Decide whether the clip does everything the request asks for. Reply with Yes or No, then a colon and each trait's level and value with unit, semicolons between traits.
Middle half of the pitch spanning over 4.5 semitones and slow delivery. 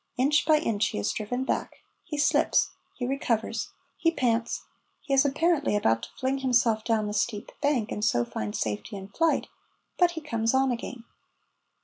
No: average, 5.1 semitones; average, 175 wpm